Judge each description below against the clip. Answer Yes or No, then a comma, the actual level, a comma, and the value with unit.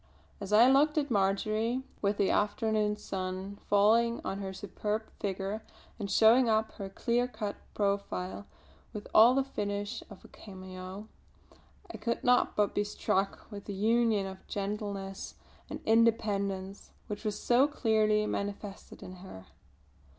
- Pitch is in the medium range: No, high, 210 Hz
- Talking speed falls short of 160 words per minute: Yes, average, 145 wpm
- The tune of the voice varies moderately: No, narrow, 2.3 semitones